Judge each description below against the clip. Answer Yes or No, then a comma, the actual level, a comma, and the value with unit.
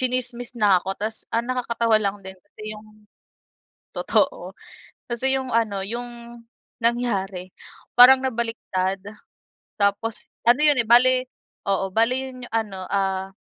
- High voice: Yes, high, 230 Hz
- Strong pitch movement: No, average, 3.7 semitones